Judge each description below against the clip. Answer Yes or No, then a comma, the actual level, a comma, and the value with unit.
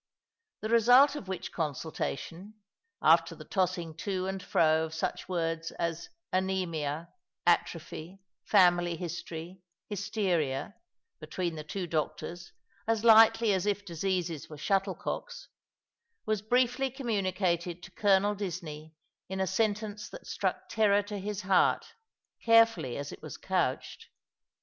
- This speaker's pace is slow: Yes, slow, 130 wpm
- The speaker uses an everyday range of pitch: Yes, average, 3.9 semitones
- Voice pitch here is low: No, high, 190 Hz